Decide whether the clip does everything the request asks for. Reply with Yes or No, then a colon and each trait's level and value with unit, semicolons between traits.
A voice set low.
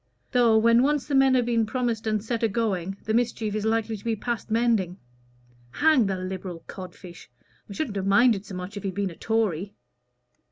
No: high, 220 Hz